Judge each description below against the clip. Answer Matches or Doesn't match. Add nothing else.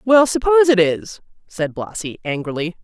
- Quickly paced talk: Doesn't match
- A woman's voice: Matches